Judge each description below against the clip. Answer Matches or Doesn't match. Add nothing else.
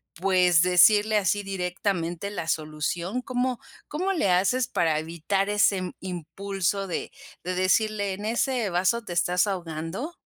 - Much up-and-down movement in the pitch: Doesn't match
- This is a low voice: Doesn't match